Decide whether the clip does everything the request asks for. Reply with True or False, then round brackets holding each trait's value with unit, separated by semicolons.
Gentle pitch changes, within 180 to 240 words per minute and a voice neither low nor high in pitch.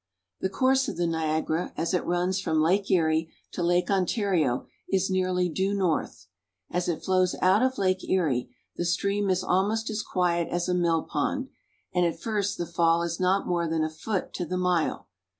True (2.3 semitones; 190 wpm; 180 Hz)